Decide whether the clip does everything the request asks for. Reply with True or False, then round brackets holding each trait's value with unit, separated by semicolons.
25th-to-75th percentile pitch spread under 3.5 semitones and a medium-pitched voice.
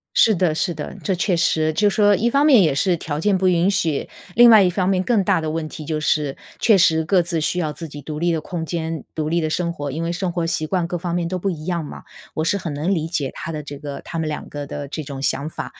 True (3.1 semitones; 165 Hz)